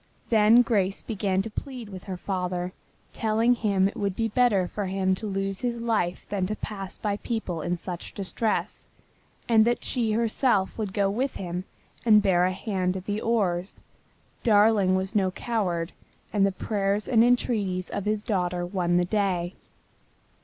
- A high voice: Yes, high, 200 Hz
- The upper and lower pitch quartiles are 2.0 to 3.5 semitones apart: Yes, average, 3.0 semitones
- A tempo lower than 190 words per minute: Yes, average, 170 wpm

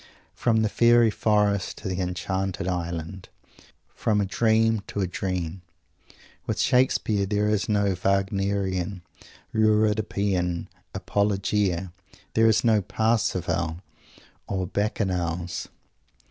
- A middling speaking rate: No, slow, 105 wpm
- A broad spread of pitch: No, average, 2.8 semitones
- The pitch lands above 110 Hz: No, low, 100 Hz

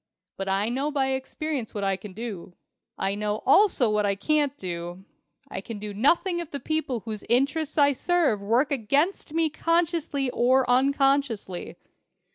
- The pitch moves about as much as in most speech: No, wide, 6.1 semitones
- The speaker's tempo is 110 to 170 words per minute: Yes, average, 160 wpm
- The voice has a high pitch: Yes, very high, 260 Hz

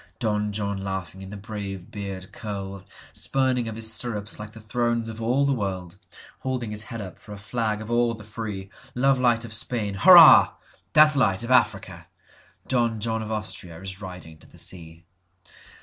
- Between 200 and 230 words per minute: No, average, 155 wpm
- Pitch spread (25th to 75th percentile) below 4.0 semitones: Yes, average, 3.2 semitones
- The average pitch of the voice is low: Yes, low, 110 Hz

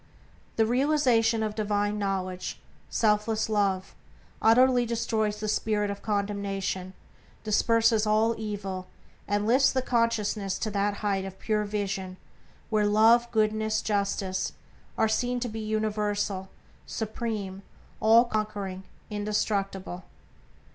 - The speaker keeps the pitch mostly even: Yes, narrow, 1.9 semitones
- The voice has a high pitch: Yes, high, 210 Hz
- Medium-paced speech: No, slow, 115 wpm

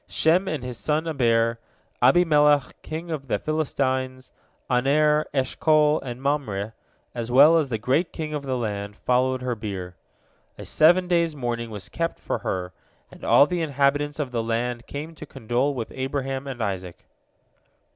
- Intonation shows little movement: No, average, 4.2 semitones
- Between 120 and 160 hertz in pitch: Yes, low, 135 Hz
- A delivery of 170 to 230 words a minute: No, average, 160 wpm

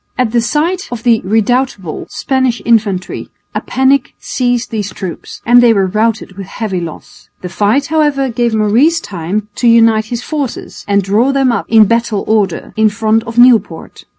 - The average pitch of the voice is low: No, high, 225 Hz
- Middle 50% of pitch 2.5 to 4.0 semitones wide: Yes, average, 3.4 semitones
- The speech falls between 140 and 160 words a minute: No, average, 175 wpm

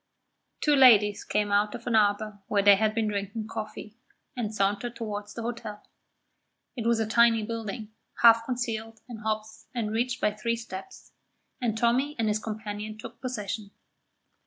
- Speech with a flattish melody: Yes, narrow, 1.9 semitones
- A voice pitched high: Yes, high, 220 Hz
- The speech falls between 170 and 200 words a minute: No, average, 160 wpm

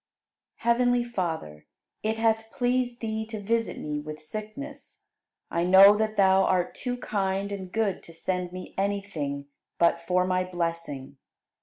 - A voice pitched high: Yes, high, 195 Hz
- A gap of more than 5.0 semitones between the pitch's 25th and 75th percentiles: No, average, 4.3 semitones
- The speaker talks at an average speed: Yes, average, 150 wpm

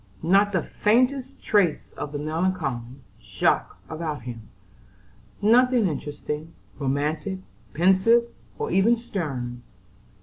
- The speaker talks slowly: Yes, slow, 100 wpm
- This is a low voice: No, medium, 170 Hz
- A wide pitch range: Yes, wide, 6.3 semitones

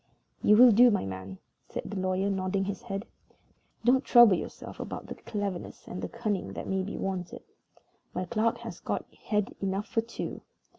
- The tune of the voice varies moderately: Yes, average, 3.2 semitones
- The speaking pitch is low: No, high, 200 Hz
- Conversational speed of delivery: Yes, average, 180 wpm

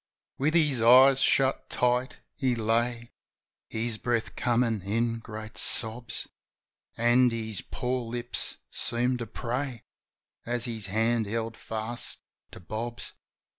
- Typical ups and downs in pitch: No, narrow, 1.7 semitones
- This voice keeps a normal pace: No, slow, 120 wpm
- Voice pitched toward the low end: Yes, low, 120 Hz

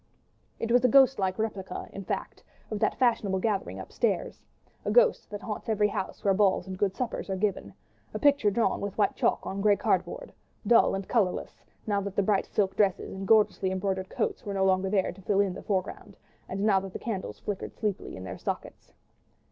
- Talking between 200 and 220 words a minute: Yes, fast, 205 wpm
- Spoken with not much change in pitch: Yes, narrow, 2.0 semitones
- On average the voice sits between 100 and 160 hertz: No, high, 200 Hz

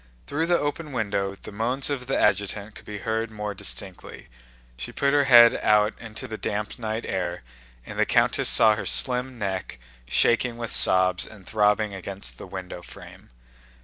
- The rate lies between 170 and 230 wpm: Yes, average, 175 wpm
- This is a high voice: No, low, 105 Hz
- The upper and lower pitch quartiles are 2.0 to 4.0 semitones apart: Yes, average, 3.4 semitones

